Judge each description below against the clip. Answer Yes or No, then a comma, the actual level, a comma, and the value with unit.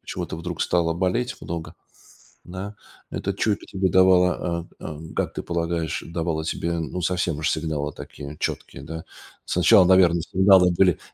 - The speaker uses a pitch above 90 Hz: No, very low, 85 Hz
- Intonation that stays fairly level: Yes, narrow, 2.3 semitones